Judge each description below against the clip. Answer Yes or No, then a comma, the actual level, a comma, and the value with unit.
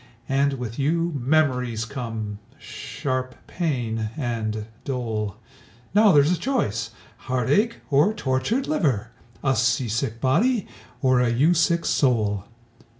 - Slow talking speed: Yes, slow, 120 wpm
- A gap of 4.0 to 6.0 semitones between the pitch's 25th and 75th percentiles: Yes, wide, 5.4 semitones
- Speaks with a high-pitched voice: No, low, 130 Hz